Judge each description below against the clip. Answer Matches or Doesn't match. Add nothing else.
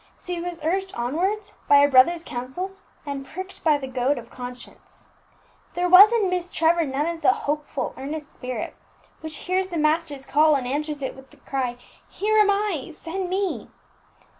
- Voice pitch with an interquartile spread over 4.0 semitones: Matches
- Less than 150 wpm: Doesn't match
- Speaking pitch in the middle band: Doesn't match